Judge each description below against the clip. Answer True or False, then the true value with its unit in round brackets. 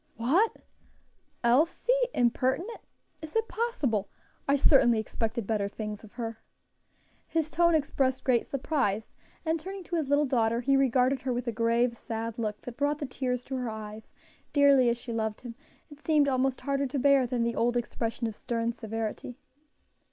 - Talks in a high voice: True (250 Hz)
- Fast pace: False (170 wpm)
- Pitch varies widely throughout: False (3.6 semitones)